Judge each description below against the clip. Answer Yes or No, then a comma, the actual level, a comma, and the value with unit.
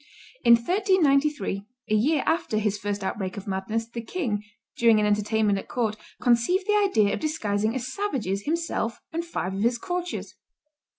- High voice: Yes, high, 230 Hz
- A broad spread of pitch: Yes, wide, 6.9 semitones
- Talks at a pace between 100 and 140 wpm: No, average, 165 wpm